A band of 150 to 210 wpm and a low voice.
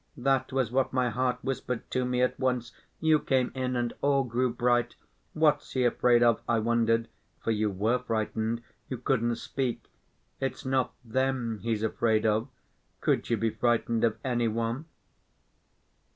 Yes: average, 155 wpm; low, 120 Hz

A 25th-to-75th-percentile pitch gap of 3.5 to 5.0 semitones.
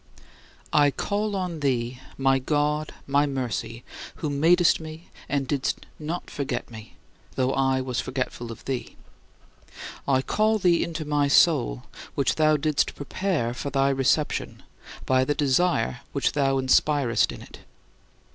No: average, 3.0 semitones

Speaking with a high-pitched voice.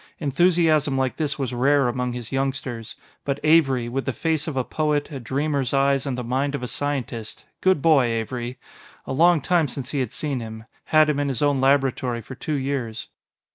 No: low, 135 Hz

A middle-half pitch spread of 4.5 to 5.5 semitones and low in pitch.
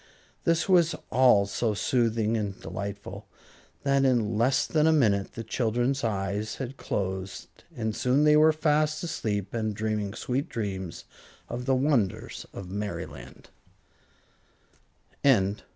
Yes: average, 5.1 semitones; low, 115 Hz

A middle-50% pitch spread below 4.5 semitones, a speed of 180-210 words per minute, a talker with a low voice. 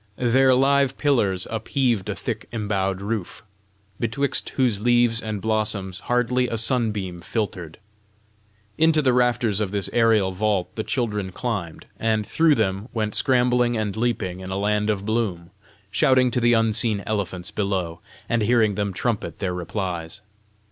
No: average, 3.8 semitones; average, 150 wpm; low, 110 Hz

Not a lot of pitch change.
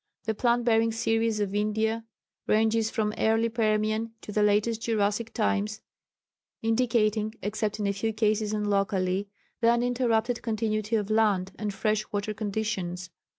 Yes: narrow, 1.4 semitones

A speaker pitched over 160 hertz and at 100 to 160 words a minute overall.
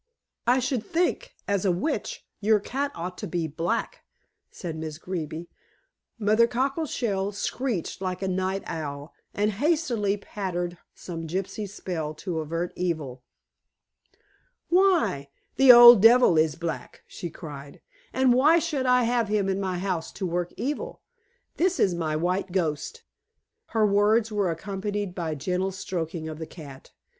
Yes: high, 190 Hz; average, 150 wpm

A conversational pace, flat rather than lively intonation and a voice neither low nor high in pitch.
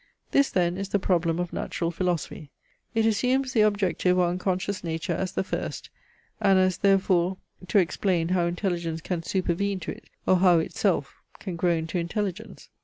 Yes: average, 170 wpm; narrow, 2.3 semitones; medium, 180 Hz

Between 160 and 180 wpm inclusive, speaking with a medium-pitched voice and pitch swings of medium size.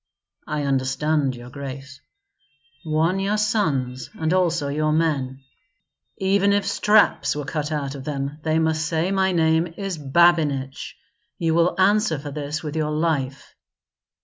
No: average, 150 wpm; medium, 155 Hz; average, 3.5 semitones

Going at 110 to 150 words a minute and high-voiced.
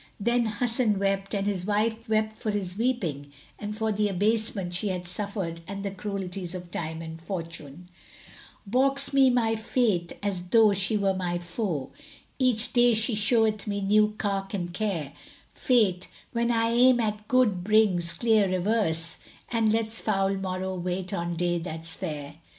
No: average, 165 wpm; high, 200 Hz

